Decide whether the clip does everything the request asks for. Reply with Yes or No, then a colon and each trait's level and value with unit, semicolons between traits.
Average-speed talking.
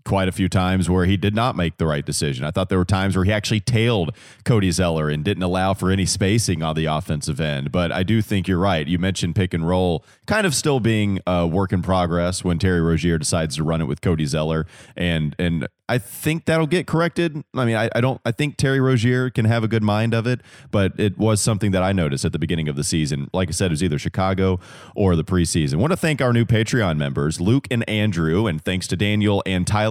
No: fast, 250 wpm